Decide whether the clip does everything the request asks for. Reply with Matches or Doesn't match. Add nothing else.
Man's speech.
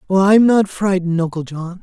Matches